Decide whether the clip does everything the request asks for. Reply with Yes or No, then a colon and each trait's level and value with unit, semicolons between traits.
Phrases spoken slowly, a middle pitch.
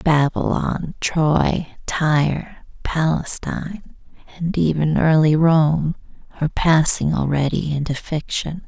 Yes: slow, 90 wpm; medium, 155 Hz